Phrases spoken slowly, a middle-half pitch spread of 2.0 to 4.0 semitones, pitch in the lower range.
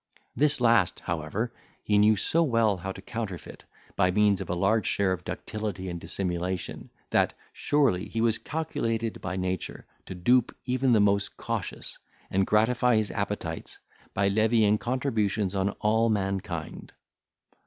No: average, 145 wpm; average, 3.5 semitones; low, 105 Hz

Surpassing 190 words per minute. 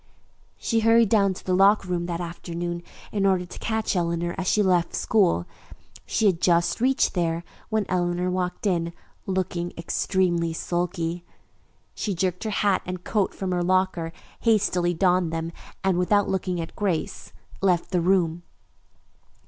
No: average, 155 wpm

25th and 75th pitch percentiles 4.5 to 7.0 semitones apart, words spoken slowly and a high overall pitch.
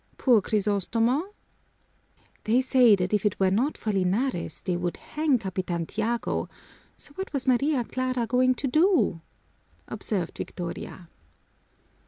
Yes: average, 5.3 semitones; slow, 130 wpm; high, 225 Hz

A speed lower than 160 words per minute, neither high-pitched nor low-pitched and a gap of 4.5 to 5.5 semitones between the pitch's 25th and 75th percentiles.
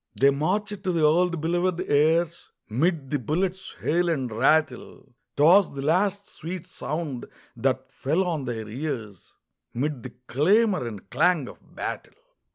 Yes: average, 145 wpm; medium, 155 Hz; average, 5.2 semitones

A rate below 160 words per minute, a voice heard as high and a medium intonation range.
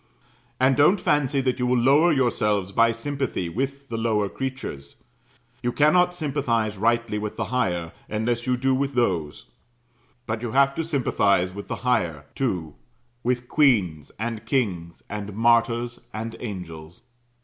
No: average, 150 wpm; low, 120 Hz; average, 4.6 semitones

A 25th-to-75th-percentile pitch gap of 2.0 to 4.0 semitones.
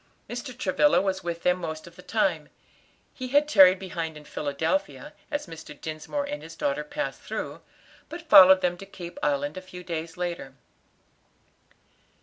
No: wide, 5.5 semitones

